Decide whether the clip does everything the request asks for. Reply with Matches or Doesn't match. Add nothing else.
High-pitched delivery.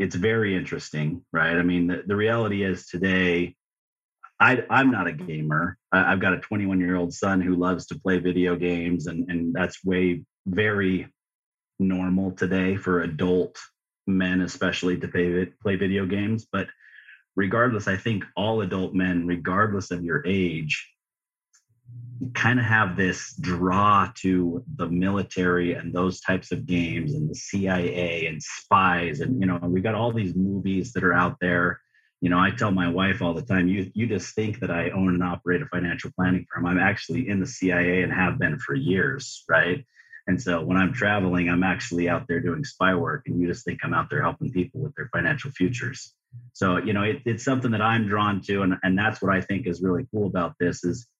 Doesn't match